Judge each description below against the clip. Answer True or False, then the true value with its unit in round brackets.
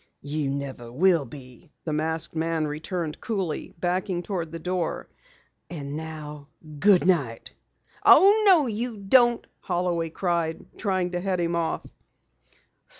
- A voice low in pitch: False (170 Hz)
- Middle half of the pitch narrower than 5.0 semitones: True (3.5 semitones)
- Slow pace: True (125 wpm)